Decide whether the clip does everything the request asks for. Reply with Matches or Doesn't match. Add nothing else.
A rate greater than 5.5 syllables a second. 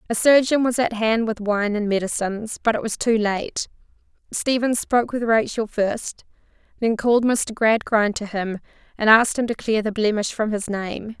Doesn't match